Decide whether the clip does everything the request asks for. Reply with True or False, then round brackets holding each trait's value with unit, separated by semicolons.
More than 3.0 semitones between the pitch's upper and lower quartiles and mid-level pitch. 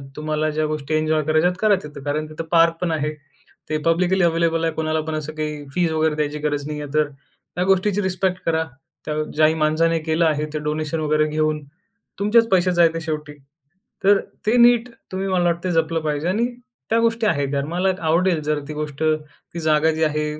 False (2.7 semitones; 160 Hz)